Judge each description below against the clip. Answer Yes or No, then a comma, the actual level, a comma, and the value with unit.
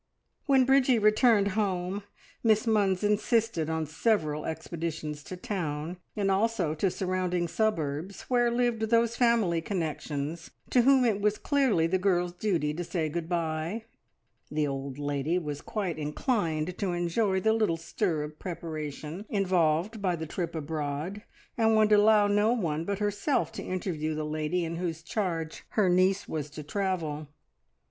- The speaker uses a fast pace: No, average, 155 wpm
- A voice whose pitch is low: No, medium, 180 Hz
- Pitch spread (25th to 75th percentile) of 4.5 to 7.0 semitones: Yes, average, 5.0 semitones